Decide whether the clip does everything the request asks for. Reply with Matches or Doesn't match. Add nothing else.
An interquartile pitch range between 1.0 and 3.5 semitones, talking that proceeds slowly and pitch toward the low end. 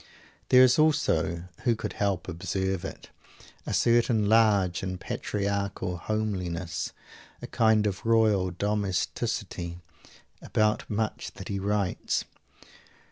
Matches